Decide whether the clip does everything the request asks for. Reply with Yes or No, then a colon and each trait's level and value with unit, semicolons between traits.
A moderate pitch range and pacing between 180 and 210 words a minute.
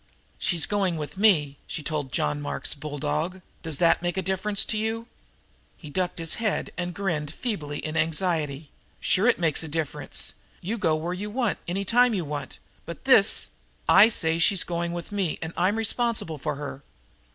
Yes: average, 4.7 semitones; average, 185 wpm